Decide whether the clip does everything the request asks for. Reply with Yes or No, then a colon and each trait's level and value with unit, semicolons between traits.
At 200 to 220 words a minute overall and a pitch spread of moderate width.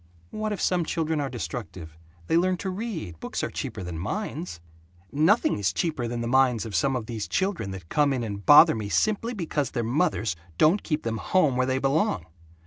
No: fast, 205 wpm; wide, 7.6 semitones